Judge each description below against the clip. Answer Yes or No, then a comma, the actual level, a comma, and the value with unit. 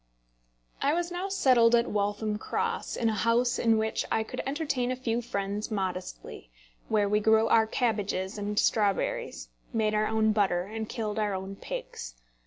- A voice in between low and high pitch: No, high, 220 Hz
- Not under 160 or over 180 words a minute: Yes, average, 170 wpm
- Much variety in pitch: No, narrow, 2.5 semitones